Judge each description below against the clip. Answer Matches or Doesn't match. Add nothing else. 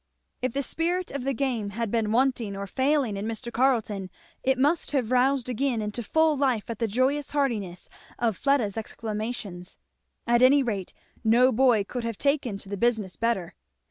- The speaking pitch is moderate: Doesn't match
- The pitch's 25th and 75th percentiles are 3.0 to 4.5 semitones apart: Matches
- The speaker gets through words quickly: Doesn't match